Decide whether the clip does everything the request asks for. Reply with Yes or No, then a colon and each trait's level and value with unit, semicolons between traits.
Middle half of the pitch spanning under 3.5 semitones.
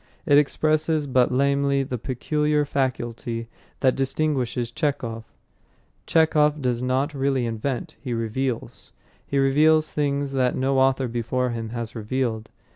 Yes: average, 3.0 semitones